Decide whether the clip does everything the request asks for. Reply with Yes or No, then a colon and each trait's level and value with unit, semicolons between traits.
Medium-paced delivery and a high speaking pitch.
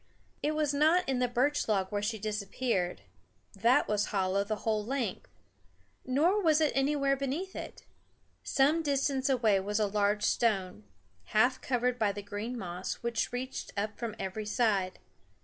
Yes: average, 160 wpm; high, 230 Hz